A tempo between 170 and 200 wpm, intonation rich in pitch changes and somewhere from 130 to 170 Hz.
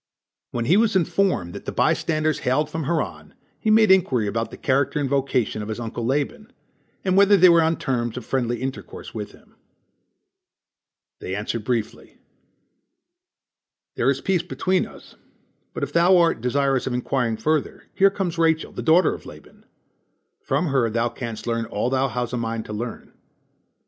Yes: average, 175 wpm; wide, 6.2 semitones; low, 135 Hz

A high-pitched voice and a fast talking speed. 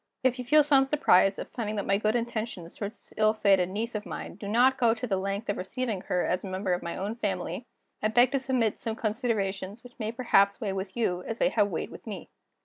Yes: high, 215 Hz; fast, 245 wpm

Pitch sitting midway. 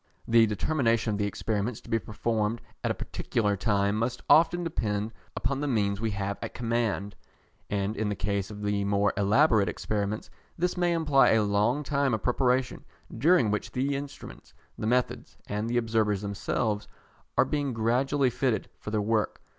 No: low, 110 Hz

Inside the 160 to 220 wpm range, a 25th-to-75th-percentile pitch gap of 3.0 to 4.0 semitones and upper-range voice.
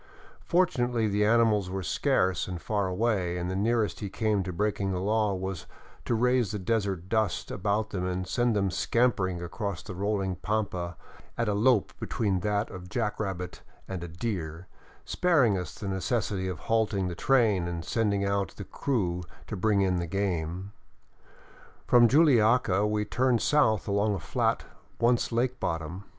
No: average, 170 wpm; average, 3.4 semitones; low, 100 Hz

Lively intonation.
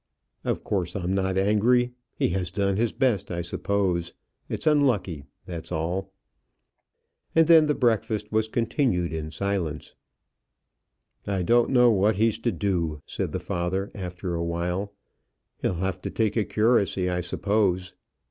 No: average, 3.9 semitones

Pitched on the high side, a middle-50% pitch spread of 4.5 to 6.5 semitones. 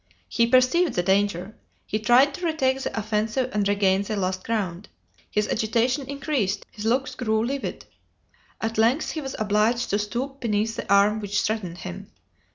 No: high, 220 Hz; average, 4.0 semitones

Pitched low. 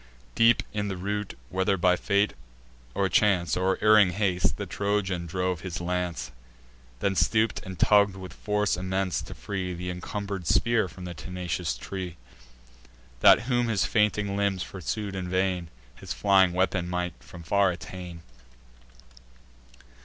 Yes: very low, 95 Hz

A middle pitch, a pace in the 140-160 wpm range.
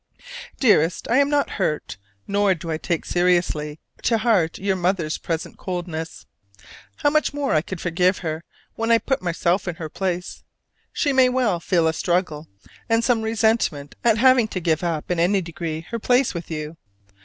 No: medium, 180 Hz; average, 175 wpm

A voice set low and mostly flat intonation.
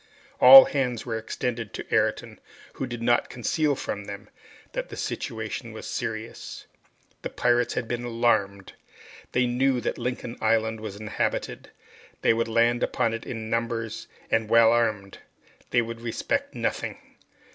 Yes: low, 115 Hz; narrow, 1.6 semitones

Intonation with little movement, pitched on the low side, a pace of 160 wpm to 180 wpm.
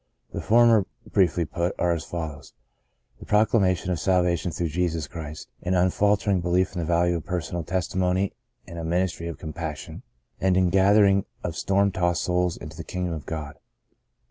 Yes: narrow, 2.1 semitones; very low, 90 Hz; average, 170 wpm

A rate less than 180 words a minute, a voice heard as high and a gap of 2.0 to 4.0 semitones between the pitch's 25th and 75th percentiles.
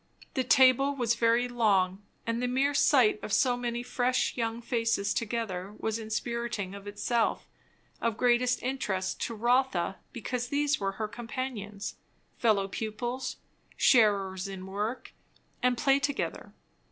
Yes: slow, 135 wpm; high, 235 Hz; average, 3.3 semitones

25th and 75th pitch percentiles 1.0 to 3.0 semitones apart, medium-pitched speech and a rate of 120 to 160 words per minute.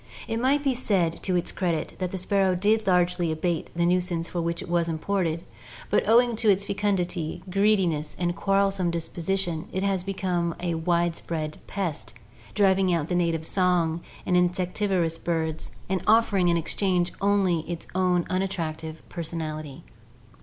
Yes: narrow, 2.6 semitones; medium, 180 Hz; average, 155 wpm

